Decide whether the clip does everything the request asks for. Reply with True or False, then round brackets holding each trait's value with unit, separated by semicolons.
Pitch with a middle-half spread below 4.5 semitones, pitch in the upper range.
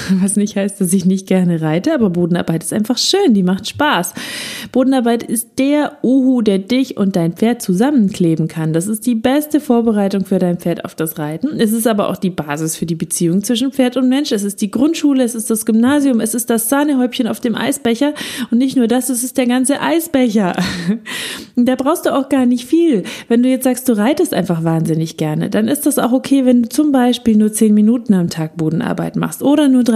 False (5.4 semitones; 235 Hz)